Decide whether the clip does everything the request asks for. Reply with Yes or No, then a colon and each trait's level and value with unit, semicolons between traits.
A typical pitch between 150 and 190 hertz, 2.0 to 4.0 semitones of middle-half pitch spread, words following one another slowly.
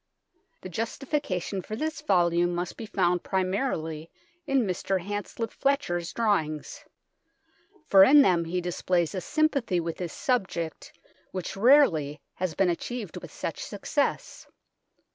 No: medium, 185 Hz; average, 5.3 semitones; slow, 125 wpm